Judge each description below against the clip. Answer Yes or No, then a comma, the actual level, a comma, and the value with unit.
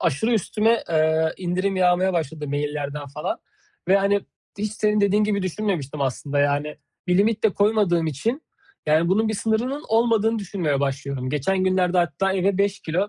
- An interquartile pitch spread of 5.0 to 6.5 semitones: Yes, wide, 5.5 semitones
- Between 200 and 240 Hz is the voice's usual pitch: No, medium, 185 Hz